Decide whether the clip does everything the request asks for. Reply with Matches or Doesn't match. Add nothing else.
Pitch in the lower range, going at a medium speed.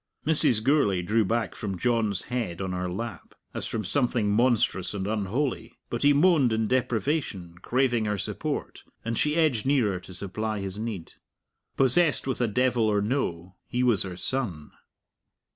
Matches